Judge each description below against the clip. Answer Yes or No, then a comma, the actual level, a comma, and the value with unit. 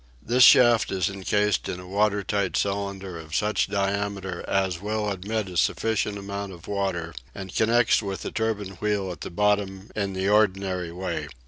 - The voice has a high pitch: No, low, 100 Hz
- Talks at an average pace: Yes, average, 175 wpm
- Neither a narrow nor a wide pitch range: No, narrow, 1.7 semitones